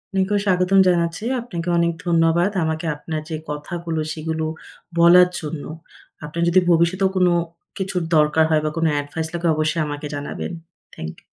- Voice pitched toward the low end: No, medium, 165 Hz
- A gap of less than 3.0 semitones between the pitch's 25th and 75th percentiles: Yes, narrow, 2.4 semitones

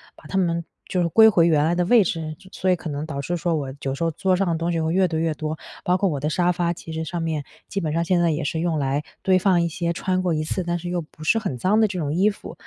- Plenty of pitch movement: No, narrow, 2.6 semitones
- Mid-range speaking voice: Yes, medium, 170 Hz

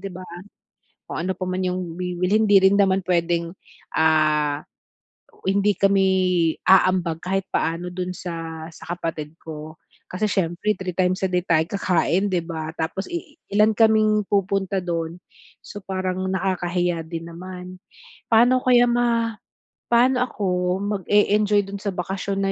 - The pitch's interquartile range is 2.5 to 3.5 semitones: Yes, average, 2.8 semitones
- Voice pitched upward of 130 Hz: Yes, medium, 185 Hz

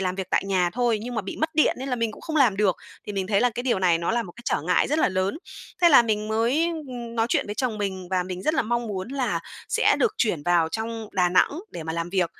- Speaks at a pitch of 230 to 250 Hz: No, high, 215 Hz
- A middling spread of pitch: Yes, average, 4.7 semitones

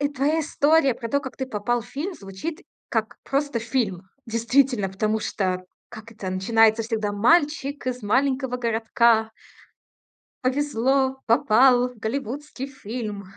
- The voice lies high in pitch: Yes, high, 240 Hz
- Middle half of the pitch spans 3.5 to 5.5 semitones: Yes, average, 3.9 semitones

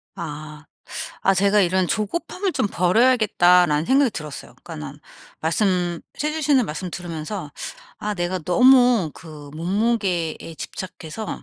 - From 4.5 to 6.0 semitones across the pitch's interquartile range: Yes, average, 5.2 semitones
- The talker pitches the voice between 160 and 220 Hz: Yes, medium, 185 Hz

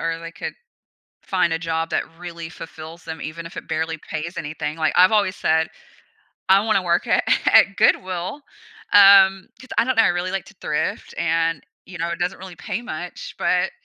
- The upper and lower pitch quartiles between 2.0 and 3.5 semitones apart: Yes, average, 2.8 semitones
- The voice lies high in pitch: No, medium, 170 Hz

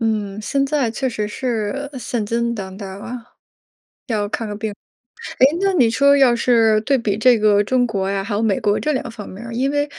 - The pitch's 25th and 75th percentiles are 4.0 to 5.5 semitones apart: No, average, 3.6 semitones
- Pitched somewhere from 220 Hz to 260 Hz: Yes, high, 225 Hz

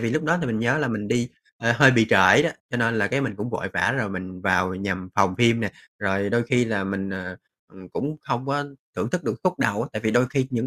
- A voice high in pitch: No, low, 115 Hz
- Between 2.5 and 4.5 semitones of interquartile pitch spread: Yes, average, 3.9 semitones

